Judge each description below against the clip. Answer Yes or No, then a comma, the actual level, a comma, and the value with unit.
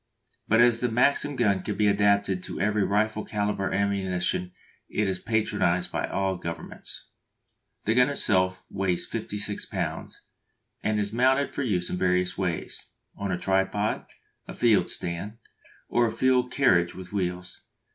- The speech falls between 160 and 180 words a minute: No, average, 150 wpm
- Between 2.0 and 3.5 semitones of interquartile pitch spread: Yes, average, 3.1 semitones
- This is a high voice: No, low, 100 Hz